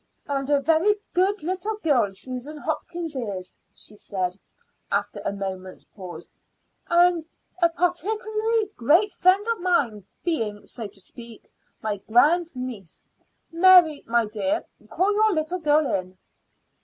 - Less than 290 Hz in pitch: No, very high, 300 Hz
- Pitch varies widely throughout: Yes, wide, 8.7 semitones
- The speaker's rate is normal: No, slow, 130 wpm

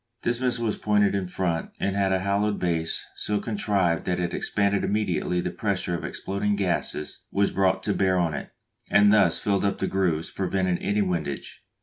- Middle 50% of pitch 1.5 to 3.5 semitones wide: Yes, narrow, 2.5 semitones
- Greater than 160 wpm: Yes, average, 190 wpm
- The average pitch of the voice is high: No, very low, 95 Hz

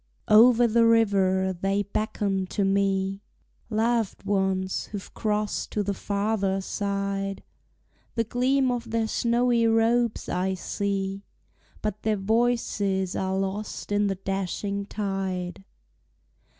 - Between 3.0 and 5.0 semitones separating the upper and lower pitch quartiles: No, narrow, 2.6 semitones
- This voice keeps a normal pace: No, slow, 115 wpm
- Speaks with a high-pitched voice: Yes, high, 200 Hz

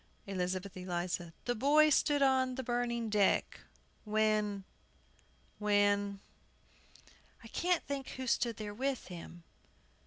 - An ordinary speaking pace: No, slow, 120 wpm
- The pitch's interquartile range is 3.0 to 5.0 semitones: Yes, average, 4.6 semitones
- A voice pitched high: Yes, high, 215 Hz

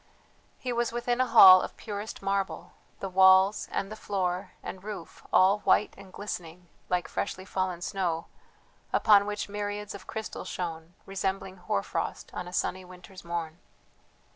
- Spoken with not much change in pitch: Yes, narrow, 2.3 semitones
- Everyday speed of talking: Yes, average, 150 wpm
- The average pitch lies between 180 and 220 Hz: Yes, high, 190 Hz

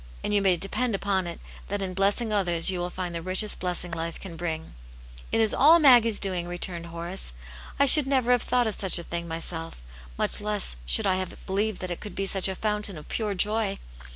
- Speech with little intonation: No, average, 3.5 semitones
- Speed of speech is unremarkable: No, fast, 235 wpm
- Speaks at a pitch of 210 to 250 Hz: No, high, 190 Hz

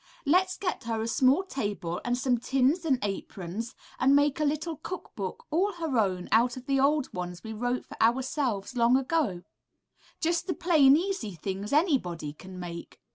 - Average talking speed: Yes, average, 180 wpm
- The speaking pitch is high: Yes, very high, 255 Hz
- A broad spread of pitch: Yes, wide, 6.9 semitones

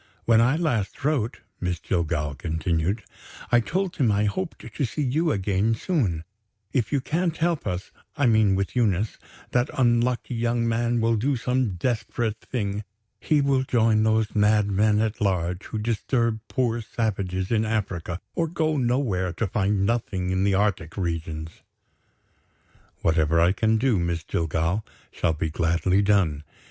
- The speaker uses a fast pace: No, average, 155 wpm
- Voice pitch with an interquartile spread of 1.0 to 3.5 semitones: No, average, 4.8 semitones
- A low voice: Yes, low, 110 Hz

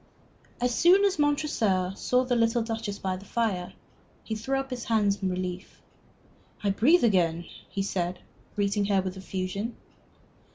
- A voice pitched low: No, high, 205 Hz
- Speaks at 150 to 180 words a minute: Yes, average, 155 wpm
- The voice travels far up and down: No, average, 4.5 semitones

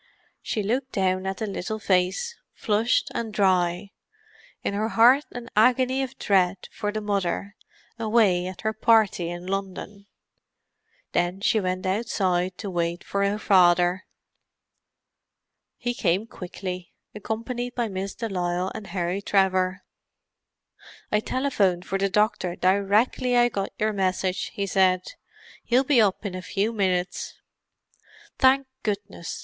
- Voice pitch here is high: Yes, high, 200 Hz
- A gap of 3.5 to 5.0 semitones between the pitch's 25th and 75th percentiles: No, average, 3.1 semitones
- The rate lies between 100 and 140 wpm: Yes, slow, 135 wpm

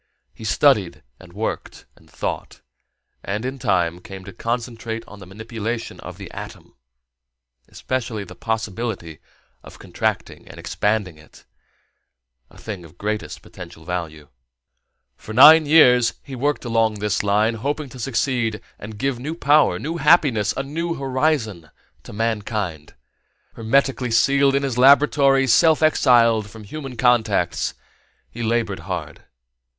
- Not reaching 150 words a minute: Yes, slow, 135 wpm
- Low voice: Yes, low, 115 Hz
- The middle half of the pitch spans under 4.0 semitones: No, average, 4.6 semitones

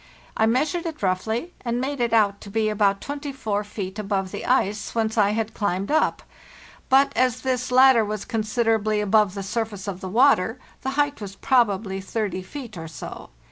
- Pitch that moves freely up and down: No, average, 4.0 semitones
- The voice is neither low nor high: No, high, 220 Hz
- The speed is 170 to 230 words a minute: Yes, average, 180 wpm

